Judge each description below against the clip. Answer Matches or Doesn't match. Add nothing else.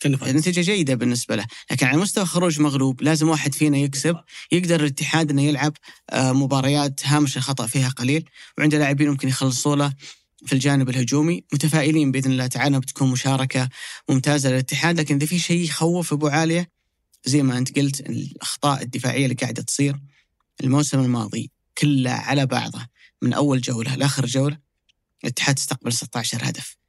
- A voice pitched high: Doesn't match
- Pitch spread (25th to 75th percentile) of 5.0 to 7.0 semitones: Doesn't match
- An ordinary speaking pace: Doesn't match